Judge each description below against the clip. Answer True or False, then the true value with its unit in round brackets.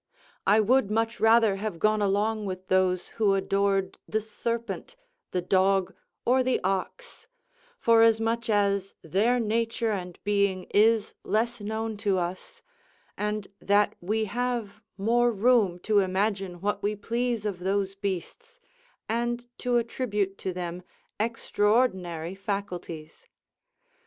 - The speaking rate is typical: False (125 wpm)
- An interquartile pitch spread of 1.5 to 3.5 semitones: True (2.9 semitones)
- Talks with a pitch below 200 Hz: False (205 Hz)